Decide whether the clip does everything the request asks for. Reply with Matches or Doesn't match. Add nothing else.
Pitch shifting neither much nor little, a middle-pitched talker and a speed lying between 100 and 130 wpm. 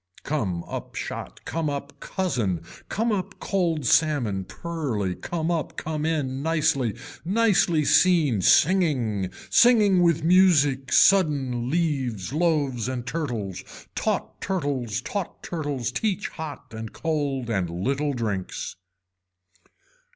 Doesn't match